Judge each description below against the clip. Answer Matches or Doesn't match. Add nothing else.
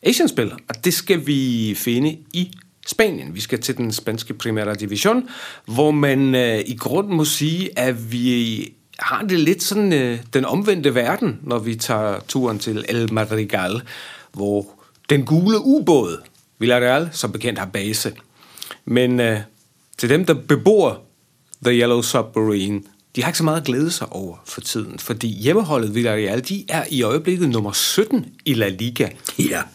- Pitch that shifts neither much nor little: Doesn't match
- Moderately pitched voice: Doesn't match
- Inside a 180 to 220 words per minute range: Doesn't match